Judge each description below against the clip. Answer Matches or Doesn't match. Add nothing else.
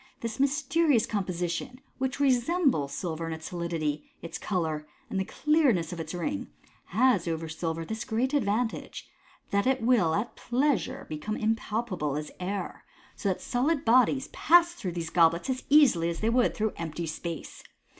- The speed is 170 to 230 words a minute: Doesn't match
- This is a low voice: Doesn't match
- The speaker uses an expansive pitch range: Matches